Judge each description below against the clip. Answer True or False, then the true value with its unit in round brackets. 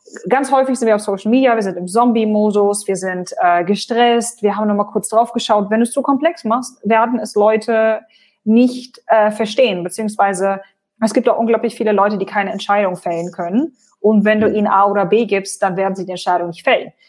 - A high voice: True (215 Hz)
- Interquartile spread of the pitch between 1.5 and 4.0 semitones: True (2.9 semitones)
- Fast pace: True (215 wpm)